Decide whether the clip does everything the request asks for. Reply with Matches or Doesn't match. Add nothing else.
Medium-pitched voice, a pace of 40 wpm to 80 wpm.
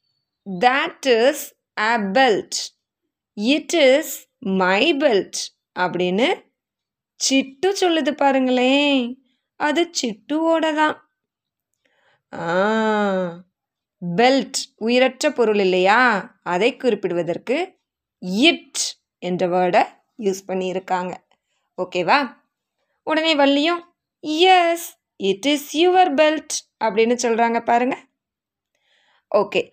Doesn't match